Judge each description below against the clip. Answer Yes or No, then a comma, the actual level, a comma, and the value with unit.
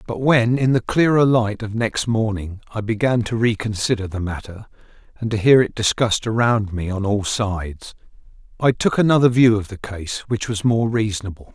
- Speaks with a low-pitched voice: Yes, low, 110 Hz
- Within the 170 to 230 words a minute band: Yes, average, 185 wpm